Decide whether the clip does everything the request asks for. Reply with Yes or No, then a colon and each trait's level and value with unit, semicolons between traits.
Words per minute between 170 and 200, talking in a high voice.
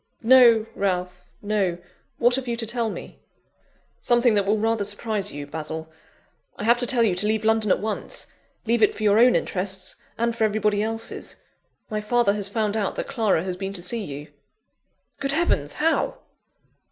Yes: average, 180 wpm; high, 215 Hz